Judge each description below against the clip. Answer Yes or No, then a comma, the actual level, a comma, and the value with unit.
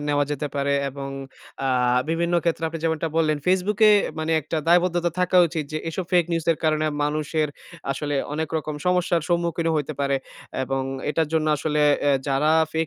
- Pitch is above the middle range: No, medium, 160 Hz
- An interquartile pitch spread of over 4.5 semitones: No, narrow, 2.4 semitones